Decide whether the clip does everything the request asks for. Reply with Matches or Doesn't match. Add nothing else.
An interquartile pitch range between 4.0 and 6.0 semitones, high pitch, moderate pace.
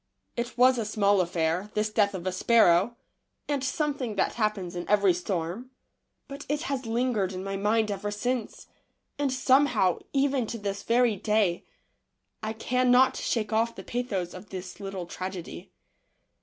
Matches